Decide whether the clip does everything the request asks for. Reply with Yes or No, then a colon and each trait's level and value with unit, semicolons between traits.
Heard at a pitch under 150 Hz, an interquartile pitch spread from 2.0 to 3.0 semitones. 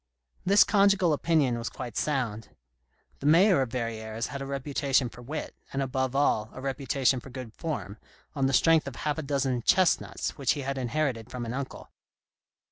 No: low, 135 Hz; average, 3.4 semitones